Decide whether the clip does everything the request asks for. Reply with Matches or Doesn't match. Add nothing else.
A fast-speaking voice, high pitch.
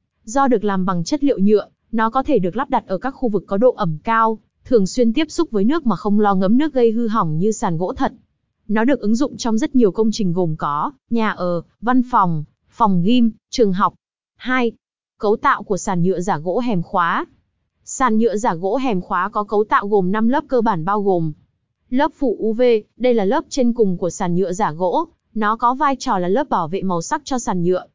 Doesn't match